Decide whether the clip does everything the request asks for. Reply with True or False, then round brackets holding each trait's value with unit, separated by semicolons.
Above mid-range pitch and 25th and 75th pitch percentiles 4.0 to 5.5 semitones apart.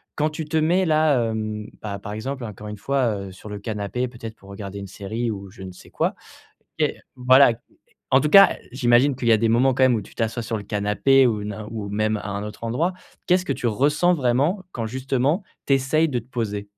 False (120 Hz; 4.5 semitones)